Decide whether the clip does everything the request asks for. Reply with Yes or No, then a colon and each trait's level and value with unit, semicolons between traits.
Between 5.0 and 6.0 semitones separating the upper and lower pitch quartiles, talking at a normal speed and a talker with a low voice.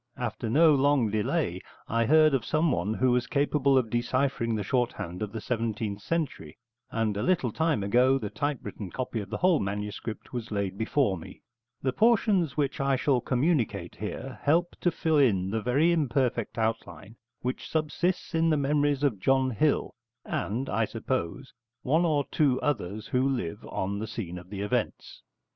Yes: average, 5.3 semitones; average, 170 wpm; low, 125 Hz